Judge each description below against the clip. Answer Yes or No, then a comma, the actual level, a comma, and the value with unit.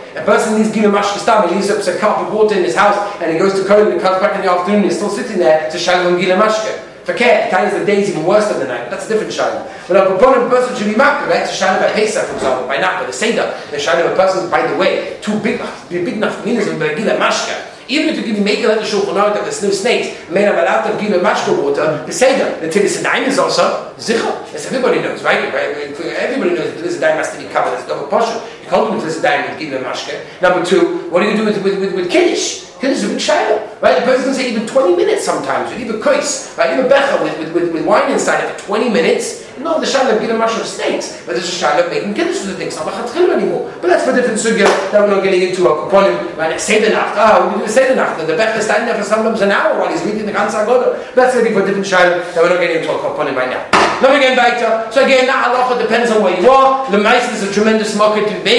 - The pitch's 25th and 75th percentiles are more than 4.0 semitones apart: Yes, average, 5.0 semitones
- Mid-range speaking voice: No, high, 215 Hz